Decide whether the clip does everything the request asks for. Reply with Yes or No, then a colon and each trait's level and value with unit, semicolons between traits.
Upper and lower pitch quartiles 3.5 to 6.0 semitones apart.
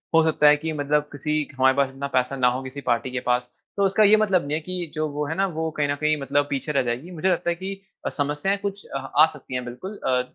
Yes: average, 4.1 semitones